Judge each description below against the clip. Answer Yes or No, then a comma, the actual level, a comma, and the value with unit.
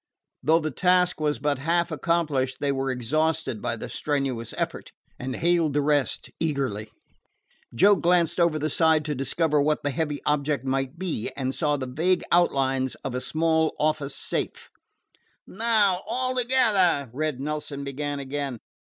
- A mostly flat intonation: No, average, 3.7 semitones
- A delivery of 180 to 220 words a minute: No, average, 155 wpm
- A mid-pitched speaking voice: Yes, medium, 150 Hz